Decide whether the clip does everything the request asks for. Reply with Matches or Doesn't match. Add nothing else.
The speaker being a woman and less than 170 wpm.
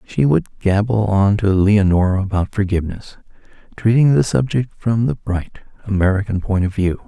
Doesn't match